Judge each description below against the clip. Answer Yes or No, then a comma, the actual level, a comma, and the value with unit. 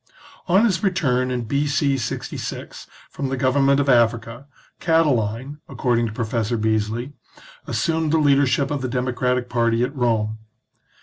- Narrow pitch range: No, average, 3.4 semitones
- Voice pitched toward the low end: Yes, low, 130 Hz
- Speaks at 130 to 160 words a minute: Yes, average, 140 wpm